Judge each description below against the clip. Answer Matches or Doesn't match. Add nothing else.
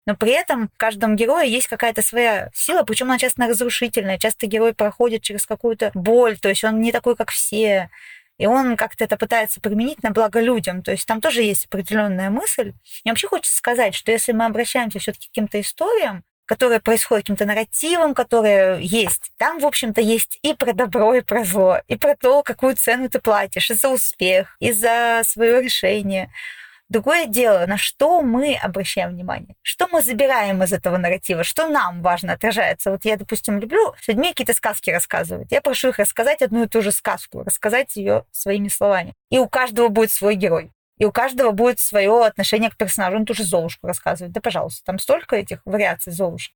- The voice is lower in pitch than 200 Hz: Doesn't match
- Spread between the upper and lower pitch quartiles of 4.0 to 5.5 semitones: Doesn't match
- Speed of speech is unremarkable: Doesn't match